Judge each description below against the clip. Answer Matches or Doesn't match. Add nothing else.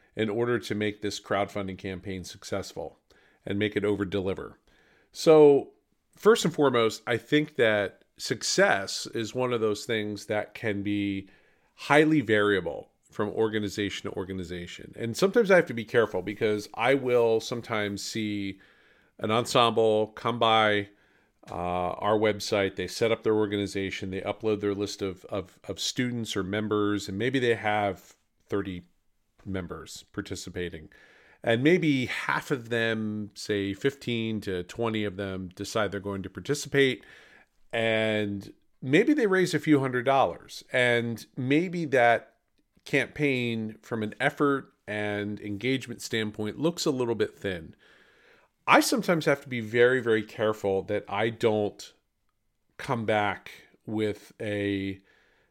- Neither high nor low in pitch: Doesn't match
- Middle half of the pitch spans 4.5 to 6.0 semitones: Doesn't match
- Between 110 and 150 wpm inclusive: Matches